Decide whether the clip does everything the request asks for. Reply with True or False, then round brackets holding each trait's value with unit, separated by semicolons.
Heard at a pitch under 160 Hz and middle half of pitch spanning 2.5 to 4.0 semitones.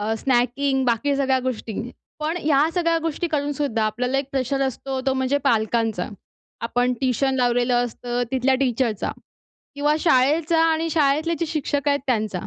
False (265 Hz; 3.1 semitones)